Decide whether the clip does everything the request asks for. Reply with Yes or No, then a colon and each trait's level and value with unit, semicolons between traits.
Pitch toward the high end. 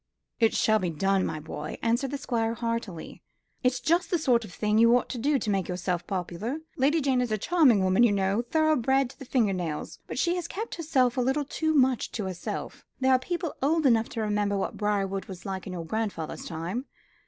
Yes: high, 230 Hz